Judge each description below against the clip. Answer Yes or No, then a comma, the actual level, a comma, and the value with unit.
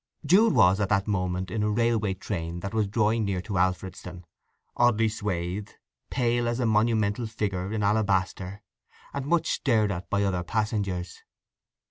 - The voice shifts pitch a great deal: No, average, 3.1 semitones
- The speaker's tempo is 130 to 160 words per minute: Yes, average, 155 wpm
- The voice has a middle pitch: No, low, 105 Hz